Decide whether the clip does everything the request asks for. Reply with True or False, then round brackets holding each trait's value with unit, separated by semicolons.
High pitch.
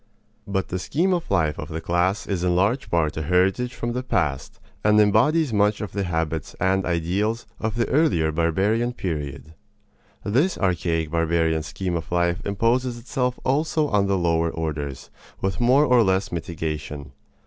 False (95 Hz)